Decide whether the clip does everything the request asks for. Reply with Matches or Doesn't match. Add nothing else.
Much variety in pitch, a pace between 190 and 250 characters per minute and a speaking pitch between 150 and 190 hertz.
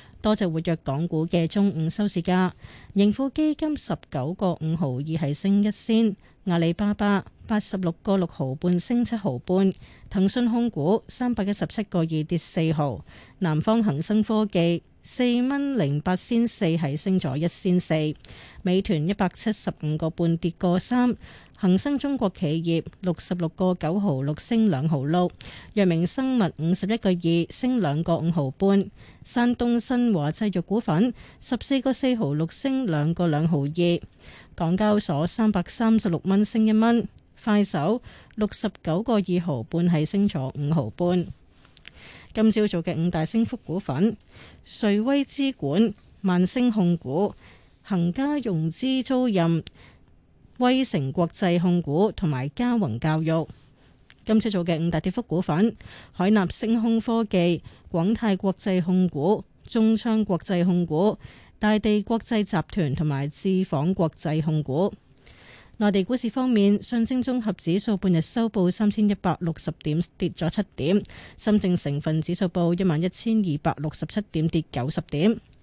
Doesn't match